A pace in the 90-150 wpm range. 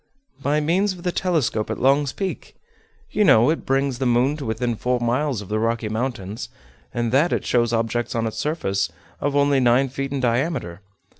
No: average, 195 wpm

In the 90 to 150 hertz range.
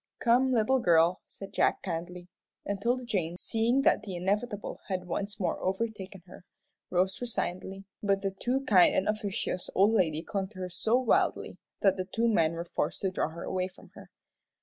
No: high, 195 Hz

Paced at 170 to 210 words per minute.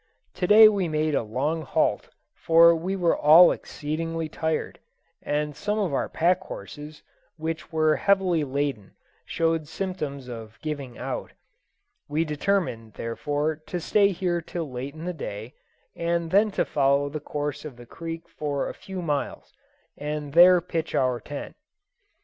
No: average, 155 wpm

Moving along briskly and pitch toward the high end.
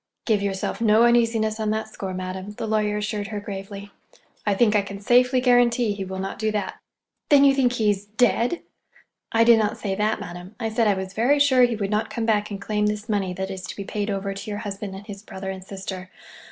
Yes: fast, 230 wpm; high, 210 Hz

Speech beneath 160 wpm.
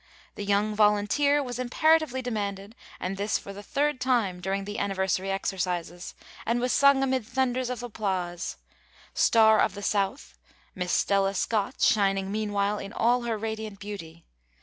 Yes: average, 150 wpm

